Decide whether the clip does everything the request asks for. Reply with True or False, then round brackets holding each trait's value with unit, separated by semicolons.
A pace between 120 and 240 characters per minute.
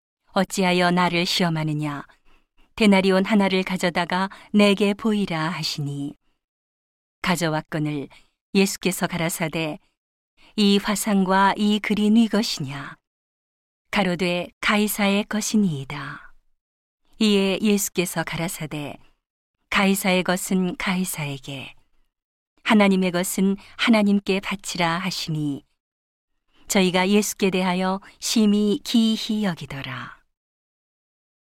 True (230 characters per minute)